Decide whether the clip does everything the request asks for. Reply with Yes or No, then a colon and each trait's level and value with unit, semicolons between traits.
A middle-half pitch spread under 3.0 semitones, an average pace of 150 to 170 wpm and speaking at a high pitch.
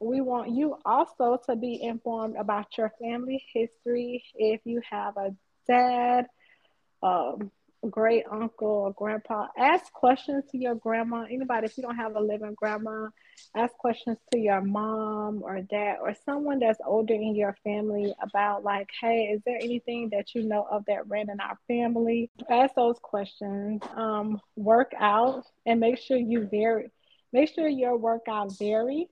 Yes: narrow, 2.6 semitones; average, 165 wpm; high, 230 Hz